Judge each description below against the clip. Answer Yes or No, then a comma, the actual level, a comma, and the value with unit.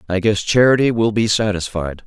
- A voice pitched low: Yes, low, 105 Hz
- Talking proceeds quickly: No, average, 175 wpm